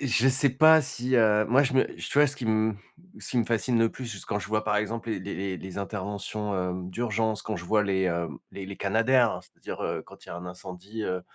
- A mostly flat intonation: No, average, 3.6 semitones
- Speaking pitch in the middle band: No, low, 110 Hz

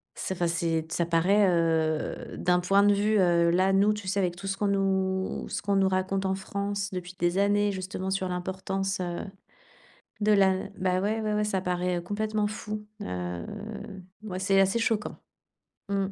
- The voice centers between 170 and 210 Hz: Yes, high, 190 Hz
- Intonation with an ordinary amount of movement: No, narrow, 2.1 semitones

